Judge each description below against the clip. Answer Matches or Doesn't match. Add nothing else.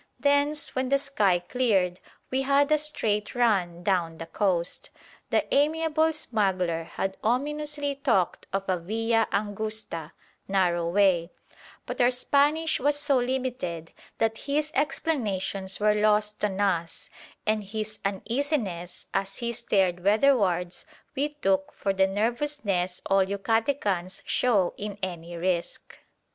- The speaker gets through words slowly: Matches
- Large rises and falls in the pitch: Matches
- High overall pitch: Matches